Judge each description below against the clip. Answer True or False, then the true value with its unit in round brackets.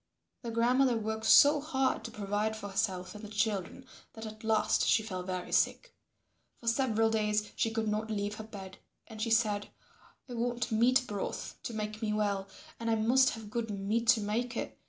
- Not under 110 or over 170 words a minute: False (195 wpm)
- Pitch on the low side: False (220 Hz)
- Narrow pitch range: True (1.9 semitones)